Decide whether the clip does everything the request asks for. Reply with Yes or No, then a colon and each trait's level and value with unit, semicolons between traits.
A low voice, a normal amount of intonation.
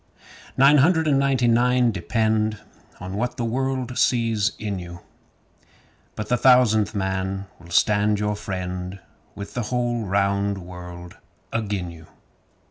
Yes: low, 105 Hz; average, 4.3 semitones